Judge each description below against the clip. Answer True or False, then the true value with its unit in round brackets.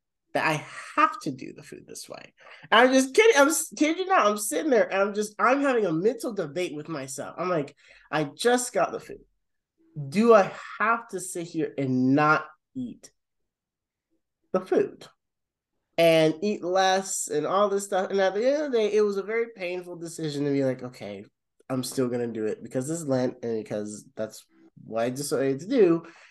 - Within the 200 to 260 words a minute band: True (205 wpm)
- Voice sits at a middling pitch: True (180 Hz)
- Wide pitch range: True (8.4 semitones)